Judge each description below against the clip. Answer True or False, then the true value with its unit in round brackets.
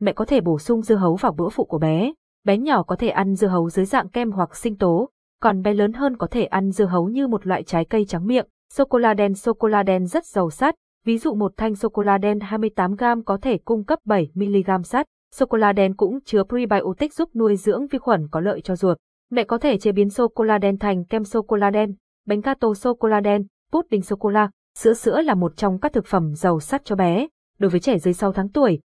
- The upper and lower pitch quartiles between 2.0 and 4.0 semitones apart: True (3.6 semitones)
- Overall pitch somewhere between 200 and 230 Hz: True (210 Hz)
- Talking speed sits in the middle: False (265 wpm)